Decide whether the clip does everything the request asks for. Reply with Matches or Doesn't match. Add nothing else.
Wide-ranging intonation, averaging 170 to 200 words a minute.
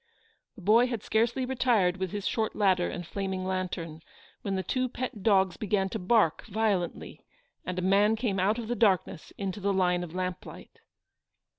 Doesn't match